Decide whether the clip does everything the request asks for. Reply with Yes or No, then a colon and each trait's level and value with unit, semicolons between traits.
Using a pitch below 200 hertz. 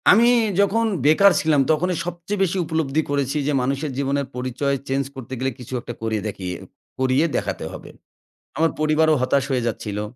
Yes: medium, 140 Hz